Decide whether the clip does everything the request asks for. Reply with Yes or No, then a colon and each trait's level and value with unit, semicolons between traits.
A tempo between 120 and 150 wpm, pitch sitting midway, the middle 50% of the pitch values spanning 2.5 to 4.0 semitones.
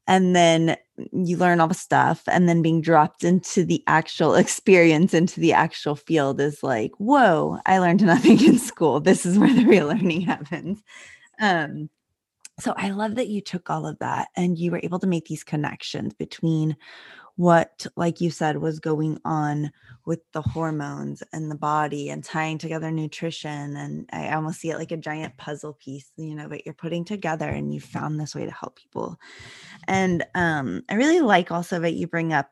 No: average, 190 wpm; medium, 165 Hz; average, 2.9 semitones